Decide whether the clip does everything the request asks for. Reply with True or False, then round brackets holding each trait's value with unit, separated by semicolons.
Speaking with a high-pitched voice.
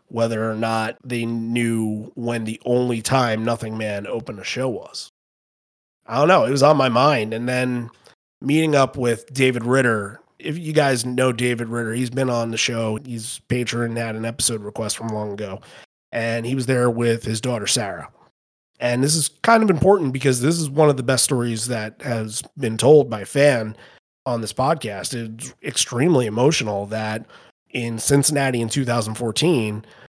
False (120 Hz)